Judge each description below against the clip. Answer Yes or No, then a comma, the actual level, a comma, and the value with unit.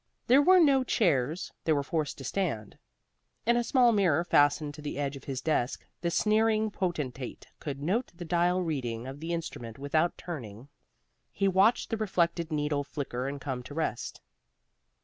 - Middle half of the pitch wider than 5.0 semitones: Yes, wide, 5.4 semitones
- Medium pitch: Yes, medium, 160 Hz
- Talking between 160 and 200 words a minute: Yes, average, 170 wpm